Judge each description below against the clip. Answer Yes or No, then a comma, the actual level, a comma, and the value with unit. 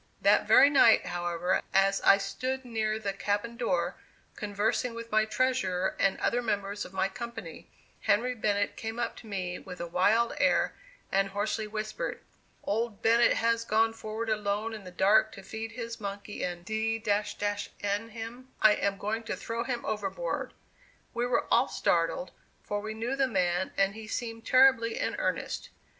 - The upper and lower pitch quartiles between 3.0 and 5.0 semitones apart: No, narrow, 2.6 semitones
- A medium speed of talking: Yes, average, 170 wpm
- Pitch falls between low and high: No, high, 220 Hz